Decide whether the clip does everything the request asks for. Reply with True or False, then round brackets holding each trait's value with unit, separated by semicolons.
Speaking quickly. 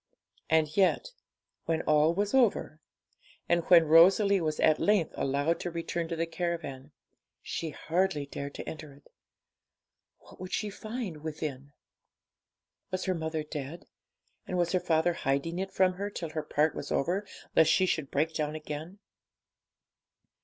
False (155 wpm)